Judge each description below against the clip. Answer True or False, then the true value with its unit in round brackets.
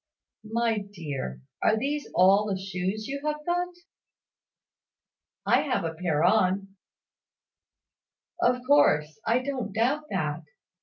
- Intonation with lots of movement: True (6.7 semitones)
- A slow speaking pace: True (115 wpm)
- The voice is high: True (215 Hz)